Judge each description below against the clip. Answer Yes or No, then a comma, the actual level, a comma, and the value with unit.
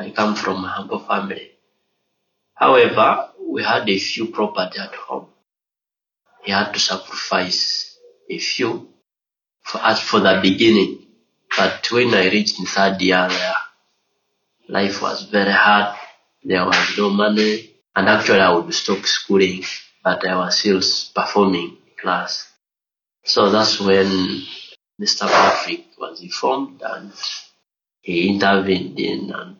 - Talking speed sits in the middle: No, slow, 130 wpm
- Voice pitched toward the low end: Yes, low, 105 Hz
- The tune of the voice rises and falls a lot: Yes, wide, 6.4 semitones